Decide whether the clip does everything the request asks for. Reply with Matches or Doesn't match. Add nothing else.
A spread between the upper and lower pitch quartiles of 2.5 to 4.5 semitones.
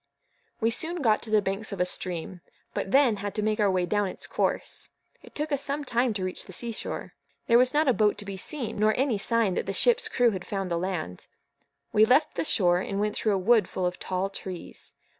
Matches